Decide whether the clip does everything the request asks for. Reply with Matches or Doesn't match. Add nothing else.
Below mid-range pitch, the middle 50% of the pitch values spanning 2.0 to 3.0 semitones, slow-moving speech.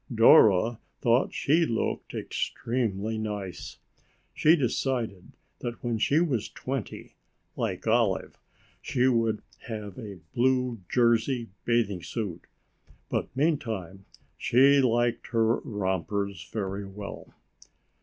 Doesn't match